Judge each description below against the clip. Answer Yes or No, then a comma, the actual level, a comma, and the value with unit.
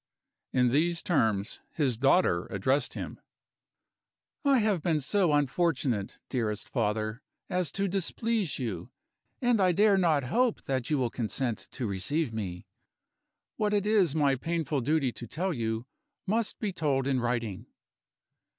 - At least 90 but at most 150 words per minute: Yes, average, 140 wpm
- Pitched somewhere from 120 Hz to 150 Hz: Yes, medium, 140 Hz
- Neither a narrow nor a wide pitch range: No, wide, 7.3 semitones